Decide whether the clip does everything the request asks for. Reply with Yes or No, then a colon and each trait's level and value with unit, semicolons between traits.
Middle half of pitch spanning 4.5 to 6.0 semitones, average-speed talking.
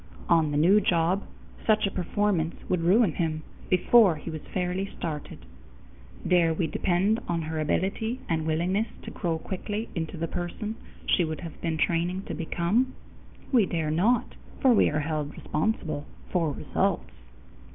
No: average, 3.7 semitones; average, 155 wpm